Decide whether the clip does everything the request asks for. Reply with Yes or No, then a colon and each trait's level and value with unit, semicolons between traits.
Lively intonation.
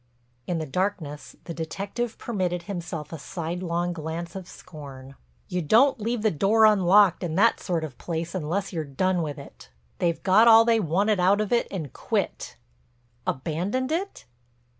No: average, 4.3 semitones